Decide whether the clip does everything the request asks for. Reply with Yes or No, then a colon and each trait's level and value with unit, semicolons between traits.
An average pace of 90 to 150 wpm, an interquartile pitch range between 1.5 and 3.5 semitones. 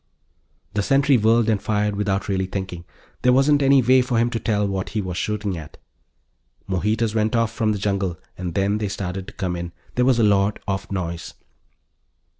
No: average, 200 wpm; average, 3.1 semitones